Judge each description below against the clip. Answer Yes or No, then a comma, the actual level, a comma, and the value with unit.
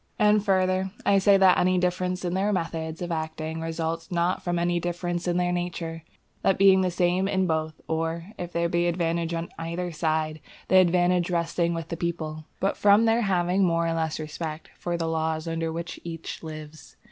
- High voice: No, medium, 170 Hz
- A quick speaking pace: No, average, 195 wpm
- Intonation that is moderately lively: No, narrow, 1.9 semitones